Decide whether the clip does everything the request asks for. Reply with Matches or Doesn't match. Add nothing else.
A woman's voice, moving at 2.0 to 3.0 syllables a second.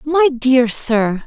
Matches